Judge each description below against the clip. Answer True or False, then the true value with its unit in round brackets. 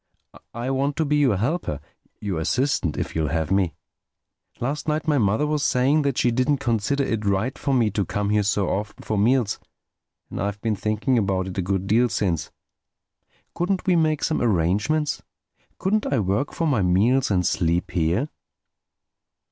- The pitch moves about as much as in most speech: False (6.4 semitones)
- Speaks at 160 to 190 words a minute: True (170 wpm)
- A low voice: True (110 Hz)